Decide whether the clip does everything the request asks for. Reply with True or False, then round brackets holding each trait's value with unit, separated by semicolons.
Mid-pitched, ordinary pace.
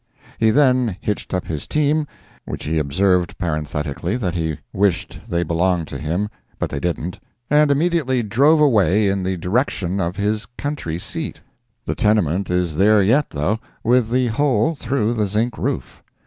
False (100 Hz; 160 wpm)